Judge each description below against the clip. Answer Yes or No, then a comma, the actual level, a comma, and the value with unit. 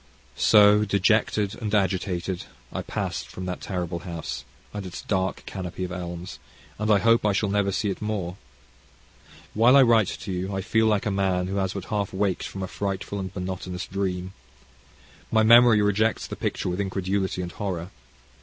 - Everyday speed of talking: Yes, average, 180 wpm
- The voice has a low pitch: Yes, very low, 95 Hz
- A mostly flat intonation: Yes, narrow, 2.3 semitones